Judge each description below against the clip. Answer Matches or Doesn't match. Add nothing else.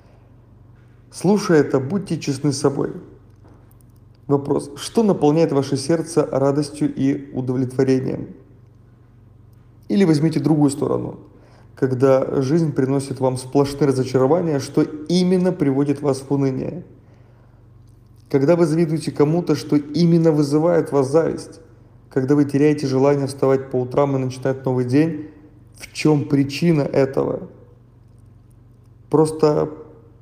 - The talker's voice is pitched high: Doesn't match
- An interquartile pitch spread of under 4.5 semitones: Matches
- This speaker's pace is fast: Doesn't match